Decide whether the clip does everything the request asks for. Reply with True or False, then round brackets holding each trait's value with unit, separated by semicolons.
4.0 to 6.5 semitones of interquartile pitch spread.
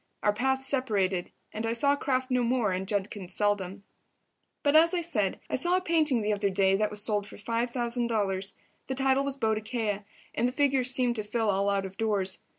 True (4.4 semitones)